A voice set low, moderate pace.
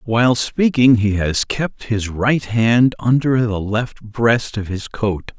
Yes: low, 115 Hz; average, 165 wpm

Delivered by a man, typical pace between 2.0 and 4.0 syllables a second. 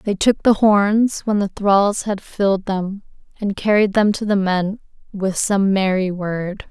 No: female; 3.9 syllables/s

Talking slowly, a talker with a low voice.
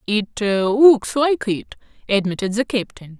No: slow, 130 wpm; high, 220 Hz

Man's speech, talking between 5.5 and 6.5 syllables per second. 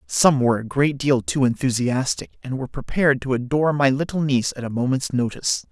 Yes: male; 6.0 syllables/s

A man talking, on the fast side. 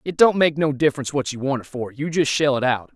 Yes: male; fast, 305 wpm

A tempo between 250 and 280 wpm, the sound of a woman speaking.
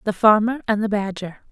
No: average, 200 wpm; female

